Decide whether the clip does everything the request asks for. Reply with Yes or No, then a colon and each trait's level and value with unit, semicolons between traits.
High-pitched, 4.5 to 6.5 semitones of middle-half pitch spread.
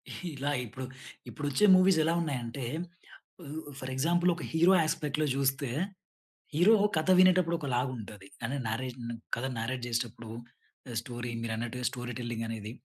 No: low, 130 Hz; average, 4.9 semitones